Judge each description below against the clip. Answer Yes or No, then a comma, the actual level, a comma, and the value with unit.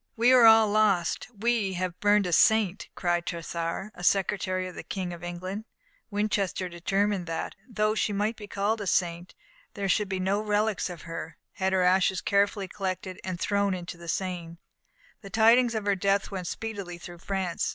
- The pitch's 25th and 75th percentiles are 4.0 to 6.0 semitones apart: No, average, 2.8 semitones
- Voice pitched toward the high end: Yes, high, 195 Hz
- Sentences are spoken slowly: No, average, 185 wpm